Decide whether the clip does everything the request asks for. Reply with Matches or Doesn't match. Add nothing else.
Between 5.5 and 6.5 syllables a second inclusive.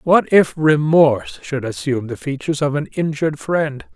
Doesn't match